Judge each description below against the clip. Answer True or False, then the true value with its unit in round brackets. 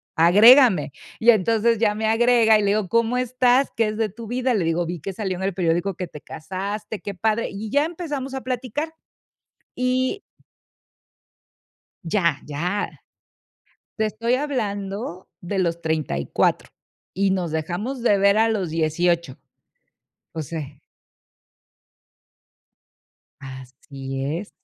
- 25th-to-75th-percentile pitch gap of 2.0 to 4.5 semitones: False (5.4 semitones)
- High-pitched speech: True (200 Hz)